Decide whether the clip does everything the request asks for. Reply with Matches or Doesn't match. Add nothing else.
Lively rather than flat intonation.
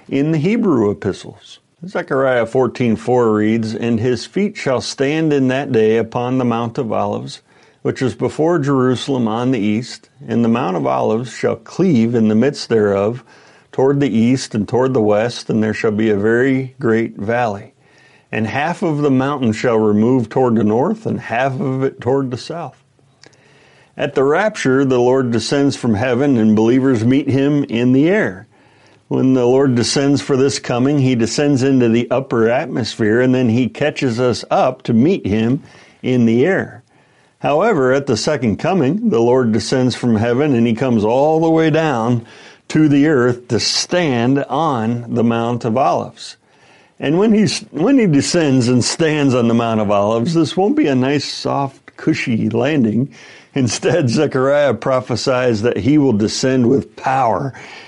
Doesn't match